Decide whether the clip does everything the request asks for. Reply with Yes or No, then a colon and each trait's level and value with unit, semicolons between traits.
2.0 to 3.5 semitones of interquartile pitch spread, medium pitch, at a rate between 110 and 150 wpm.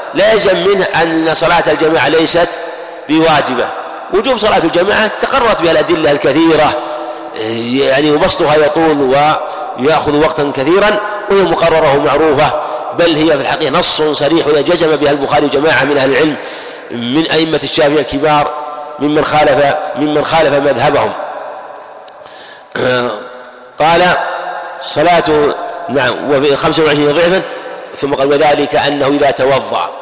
Yes: narrow, 2.5 semitones; medium, 150 Hz; average, 115 wpm